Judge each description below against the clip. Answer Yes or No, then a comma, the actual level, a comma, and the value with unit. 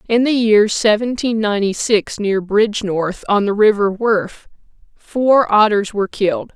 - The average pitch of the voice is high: Yes, high, 210 Hz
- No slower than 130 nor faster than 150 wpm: Yes, average, 145 wpm